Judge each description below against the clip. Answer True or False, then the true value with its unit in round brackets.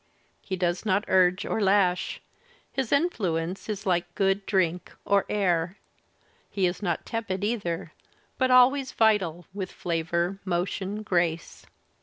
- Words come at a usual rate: False (125 wpm)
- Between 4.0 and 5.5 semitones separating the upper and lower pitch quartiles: False (3.1 semitones)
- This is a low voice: False (190 Hz)